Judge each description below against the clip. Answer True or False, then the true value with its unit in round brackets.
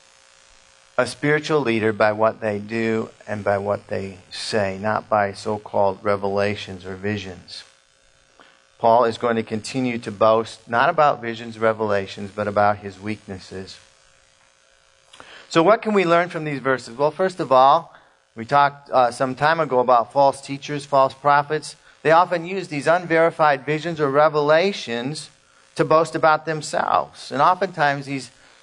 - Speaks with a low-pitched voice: True (115 Hz)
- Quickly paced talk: False (150 wpm)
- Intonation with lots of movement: True (6.7 semitones)